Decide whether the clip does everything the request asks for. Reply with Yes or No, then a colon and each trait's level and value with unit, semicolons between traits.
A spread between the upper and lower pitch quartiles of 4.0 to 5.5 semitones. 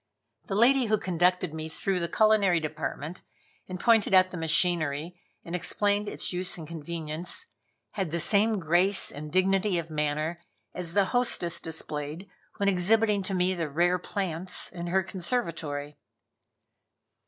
No: average, 3.4 semitones